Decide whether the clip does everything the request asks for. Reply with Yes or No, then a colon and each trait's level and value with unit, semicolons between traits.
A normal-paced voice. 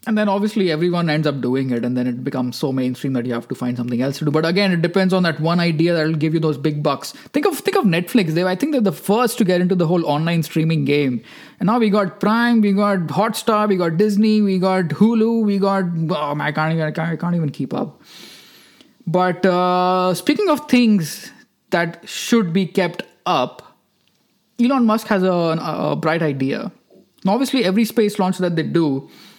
No: fast, 225 wpm